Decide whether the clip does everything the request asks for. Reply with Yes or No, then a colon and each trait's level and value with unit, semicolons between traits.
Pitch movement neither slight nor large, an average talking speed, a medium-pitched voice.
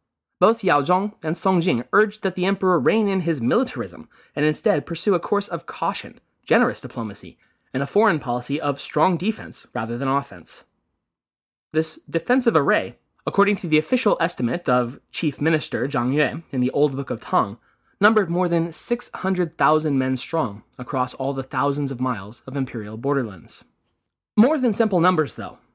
No: wide, 6.1 semitones; average, 170 wpm; medium, 155 Hz